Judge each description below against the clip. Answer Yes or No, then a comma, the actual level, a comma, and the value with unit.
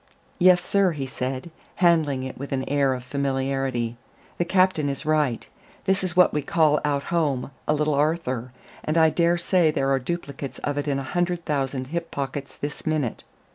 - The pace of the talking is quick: No, average, 185 wpm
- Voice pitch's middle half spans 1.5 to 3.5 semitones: No, average, 3.9 semitones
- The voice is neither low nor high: Yes, medium, 145 Hz